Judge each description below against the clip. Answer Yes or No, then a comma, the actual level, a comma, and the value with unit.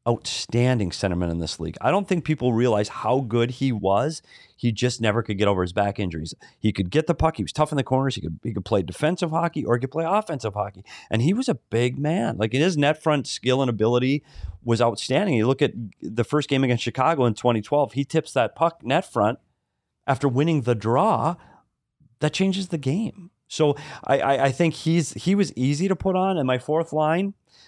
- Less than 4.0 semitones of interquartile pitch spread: No, average, 5.1 semitones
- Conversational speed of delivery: No, fast, 220 wpm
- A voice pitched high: No, low, 130 Hz